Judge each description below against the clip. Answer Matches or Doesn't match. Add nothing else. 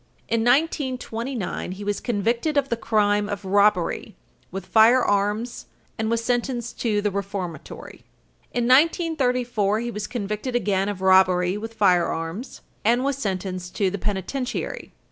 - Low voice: Doesn't match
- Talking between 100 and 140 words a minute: Matches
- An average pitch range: Matches